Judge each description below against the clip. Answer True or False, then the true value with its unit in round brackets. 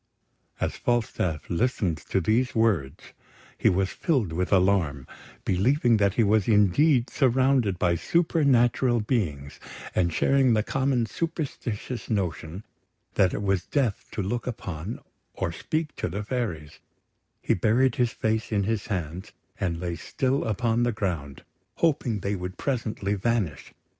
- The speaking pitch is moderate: False (105 Hz)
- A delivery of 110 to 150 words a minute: True (140 wpm)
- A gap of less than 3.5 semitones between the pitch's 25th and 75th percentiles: False (5.2 semitones)